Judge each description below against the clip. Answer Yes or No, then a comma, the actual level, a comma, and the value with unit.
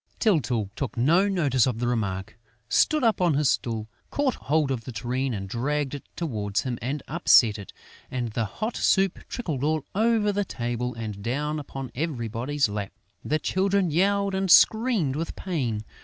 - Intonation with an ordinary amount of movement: No, wide, 7.4 semitones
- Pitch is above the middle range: No, medium, 140 Hz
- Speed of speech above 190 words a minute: No, average, 170 wpm